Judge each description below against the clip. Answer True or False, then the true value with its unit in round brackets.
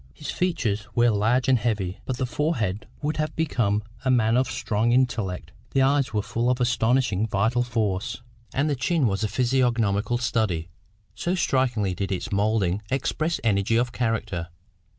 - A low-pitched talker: True (115 Hz)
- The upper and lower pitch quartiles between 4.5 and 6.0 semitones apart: False (4.0 semitones)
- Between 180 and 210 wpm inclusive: False (165 wpm)